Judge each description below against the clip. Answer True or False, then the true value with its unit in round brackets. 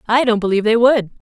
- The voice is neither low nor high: False (225 Hz)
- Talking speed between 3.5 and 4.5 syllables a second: False (7.0 syllables/s)